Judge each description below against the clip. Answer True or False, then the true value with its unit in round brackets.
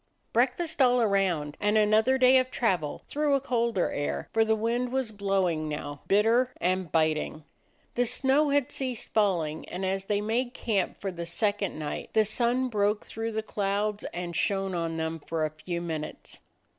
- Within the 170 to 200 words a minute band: True (175 wpm)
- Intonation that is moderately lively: False (5.8 semitones)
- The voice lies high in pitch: True (210 Hz)